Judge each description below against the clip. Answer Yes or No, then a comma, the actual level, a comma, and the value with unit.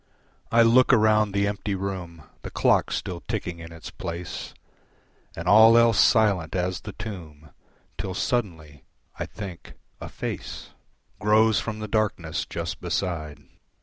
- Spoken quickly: No, average, 140 wpm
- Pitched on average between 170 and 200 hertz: No, low, 100 Hz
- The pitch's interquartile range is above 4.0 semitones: Yes, average, 4.4 semitones